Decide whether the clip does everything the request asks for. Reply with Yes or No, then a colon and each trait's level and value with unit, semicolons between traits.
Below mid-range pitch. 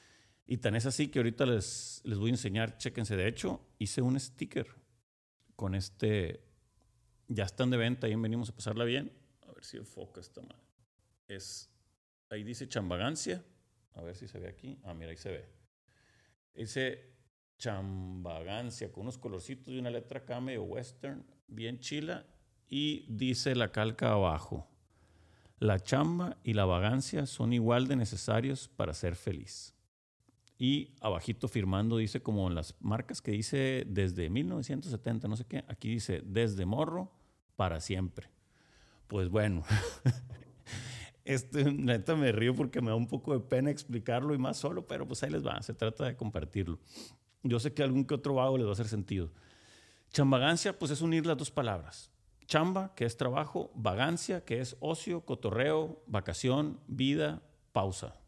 Yes: low, 115 Hz